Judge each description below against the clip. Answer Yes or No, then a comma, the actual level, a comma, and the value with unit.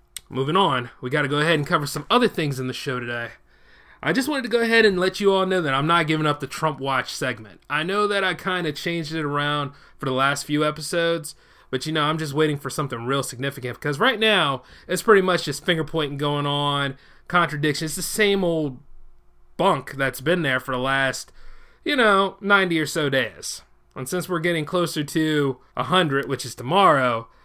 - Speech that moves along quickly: Yes, fast, 215 wpm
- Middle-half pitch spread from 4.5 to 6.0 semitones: Yes, average, 4.8 semitones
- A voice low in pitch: No, medium, 150 Hz